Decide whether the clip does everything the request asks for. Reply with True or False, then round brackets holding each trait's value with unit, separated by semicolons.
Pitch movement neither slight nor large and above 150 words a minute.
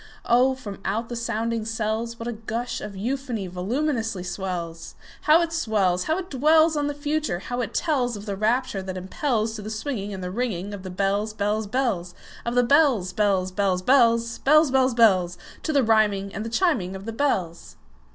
True (4.8 semitones; 160 wpm)